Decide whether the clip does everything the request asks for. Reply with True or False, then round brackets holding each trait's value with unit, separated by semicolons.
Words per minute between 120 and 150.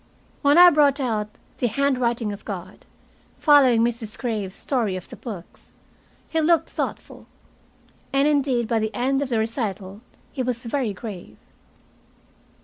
True (145 wpm)